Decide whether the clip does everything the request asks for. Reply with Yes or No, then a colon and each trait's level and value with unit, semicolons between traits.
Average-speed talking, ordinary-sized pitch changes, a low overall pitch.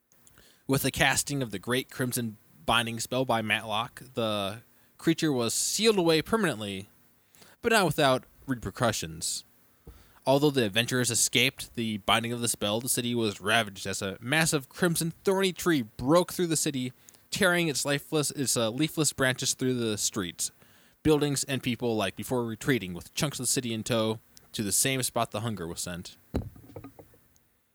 Yes: average, 160 wpm; average, 4.1 semitones; low, 120 Hz